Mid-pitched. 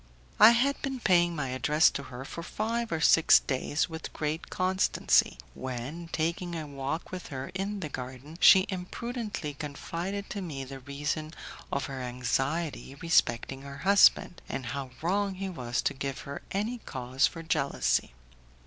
Yes: medium, 155 Hz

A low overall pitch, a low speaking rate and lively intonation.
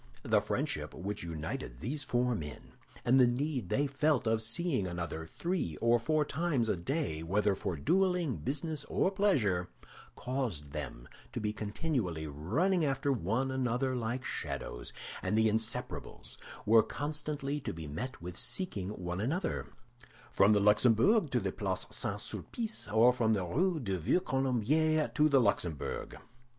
No: low, 120 Hz; average, 155 wpm; wide, 7.4 semitones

